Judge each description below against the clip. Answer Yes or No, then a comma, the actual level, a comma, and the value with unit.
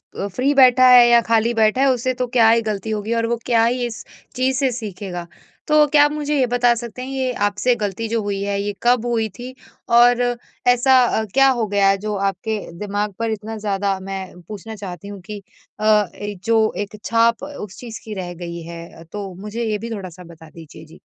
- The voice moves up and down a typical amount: Yes, average, 3.5 semitones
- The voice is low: No, high, 225 Hz